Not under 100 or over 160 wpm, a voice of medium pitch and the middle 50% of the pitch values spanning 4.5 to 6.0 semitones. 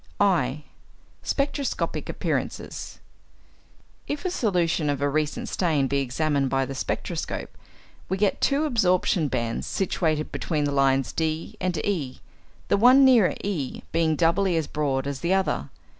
Yes: average, 145 wpm; medium, 160 Hz; wide, 5.5 semitones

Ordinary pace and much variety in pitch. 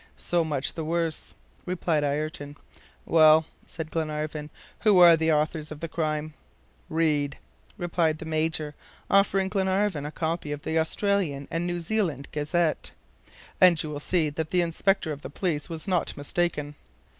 No: average, 155 wpm; narrow, 2.4 semitones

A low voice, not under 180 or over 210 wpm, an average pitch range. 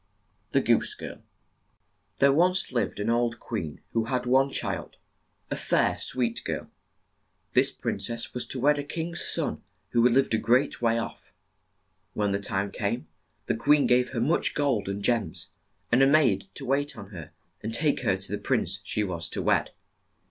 Yes: low, 120 Hz; average, 185 wpm; average, 4.7 semitones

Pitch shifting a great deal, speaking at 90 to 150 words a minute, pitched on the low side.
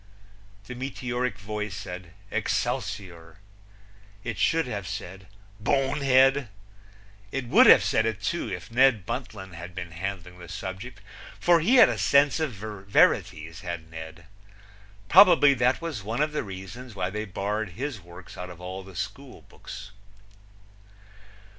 Yes: wide, 5.8 semitones; average, 140 wpm; low, 105 Hz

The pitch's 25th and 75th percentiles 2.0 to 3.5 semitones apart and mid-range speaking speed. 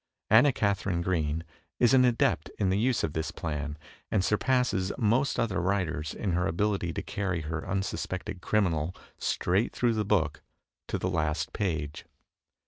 No: average, 4.5 semitones; average, 155 wpm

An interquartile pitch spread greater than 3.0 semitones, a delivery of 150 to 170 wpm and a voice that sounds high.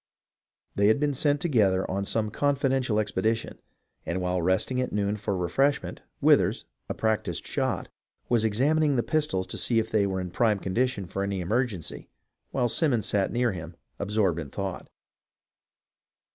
No: average, 5.0 semitones; average, 160 wpm; low, 110 Hz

